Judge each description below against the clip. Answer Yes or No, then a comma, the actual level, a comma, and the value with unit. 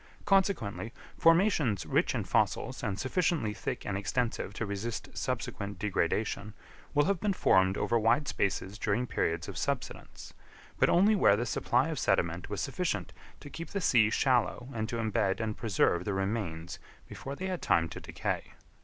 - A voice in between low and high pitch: No, low, 110 Hz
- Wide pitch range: Yes, wide, 6.4 semitones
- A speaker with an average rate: Yes, average, 165 wpm